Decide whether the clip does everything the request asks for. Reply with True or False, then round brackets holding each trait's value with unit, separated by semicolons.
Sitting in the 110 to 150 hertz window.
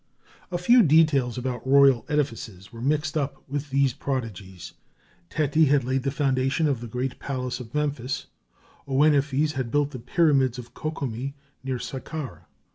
True (135 Hz)